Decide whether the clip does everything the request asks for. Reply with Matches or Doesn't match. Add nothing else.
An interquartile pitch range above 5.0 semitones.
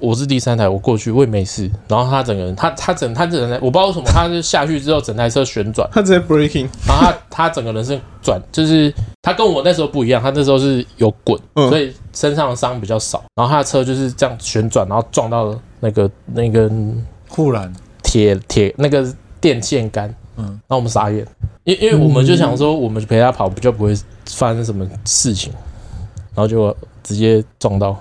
Doesn't match